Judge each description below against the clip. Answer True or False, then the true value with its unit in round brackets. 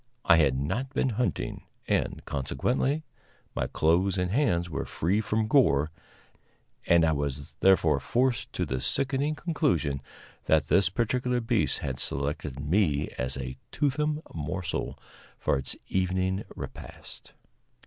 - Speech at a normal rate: False (130 wpm)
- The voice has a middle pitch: False (90 Hz)